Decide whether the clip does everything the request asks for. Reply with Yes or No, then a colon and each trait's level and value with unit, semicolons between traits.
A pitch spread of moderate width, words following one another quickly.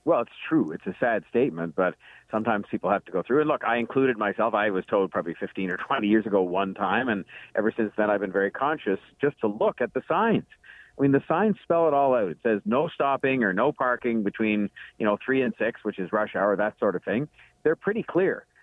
Yes: average, 4.8 semitones; fast, 245 wpm